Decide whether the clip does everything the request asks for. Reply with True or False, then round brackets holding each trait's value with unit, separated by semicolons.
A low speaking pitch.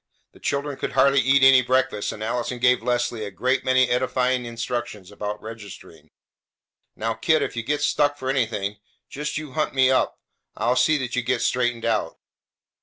True (125 Hz)